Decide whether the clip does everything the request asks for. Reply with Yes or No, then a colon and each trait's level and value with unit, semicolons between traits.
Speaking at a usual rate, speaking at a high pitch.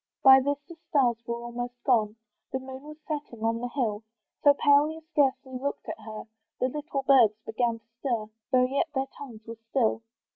Yes: average, 190 wpm; very high, 255 Hz